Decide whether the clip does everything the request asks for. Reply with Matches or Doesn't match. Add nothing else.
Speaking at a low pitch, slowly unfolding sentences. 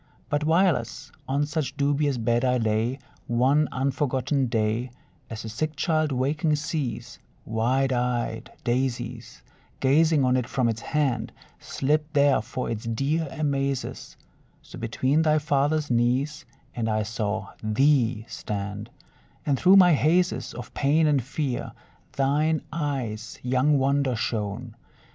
Matches